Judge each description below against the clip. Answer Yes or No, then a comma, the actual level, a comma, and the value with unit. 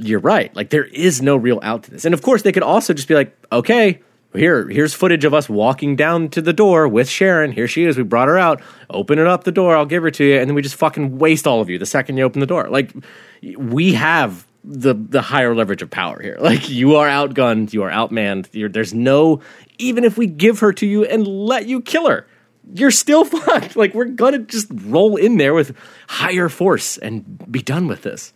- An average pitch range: No, wide, 8.1 semitones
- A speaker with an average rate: No, fast, 240 wpm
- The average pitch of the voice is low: No, medium, 155 Hz